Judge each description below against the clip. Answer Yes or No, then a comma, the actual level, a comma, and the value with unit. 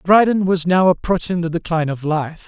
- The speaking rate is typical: Yes, average, 195 wpm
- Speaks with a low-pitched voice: No, medium, 175 Hz